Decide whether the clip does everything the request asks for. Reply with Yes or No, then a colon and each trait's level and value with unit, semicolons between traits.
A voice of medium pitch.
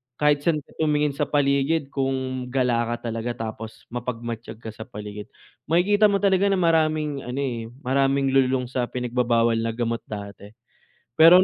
No: low, 130 Hz